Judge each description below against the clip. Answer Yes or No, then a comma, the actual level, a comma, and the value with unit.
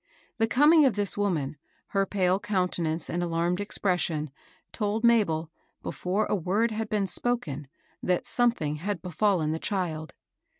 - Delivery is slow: No, average, 155 wpm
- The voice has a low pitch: No, medium, 185 Hz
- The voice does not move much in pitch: No, average, 4.4 semitones